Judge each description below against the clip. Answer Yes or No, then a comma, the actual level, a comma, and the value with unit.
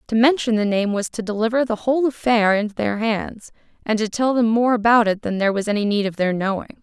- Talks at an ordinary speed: No, fast, 245 wpm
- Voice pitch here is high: Yes, high, 220 Hz